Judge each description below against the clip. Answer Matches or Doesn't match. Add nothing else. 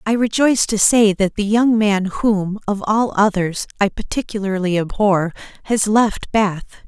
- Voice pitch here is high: Matches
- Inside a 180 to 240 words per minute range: Doesn't match